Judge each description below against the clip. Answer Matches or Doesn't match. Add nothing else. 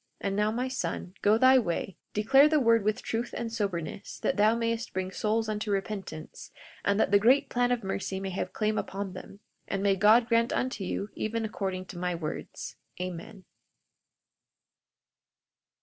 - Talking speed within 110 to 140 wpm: Doesn't match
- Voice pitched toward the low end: Doesn't match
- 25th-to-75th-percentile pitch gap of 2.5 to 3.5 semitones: Matches